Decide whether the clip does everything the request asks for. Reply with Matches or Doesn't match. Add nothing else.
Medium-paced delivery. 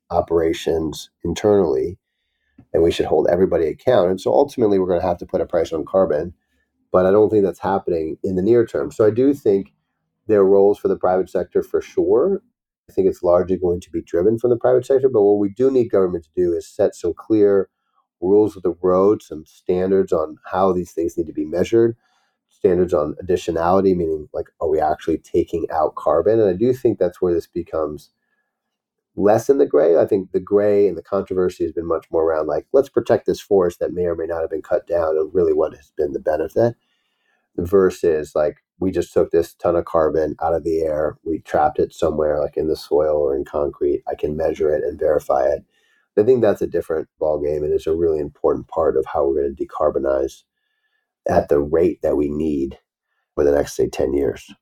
Doesn't match